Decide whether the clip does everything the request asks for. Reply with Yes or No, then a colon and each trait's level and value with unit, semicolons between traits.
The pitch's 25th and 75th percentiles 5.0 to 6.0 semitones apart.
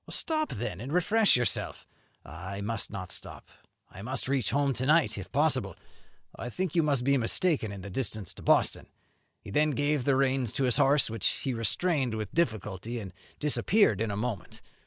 Yes: average, 5.3 semitones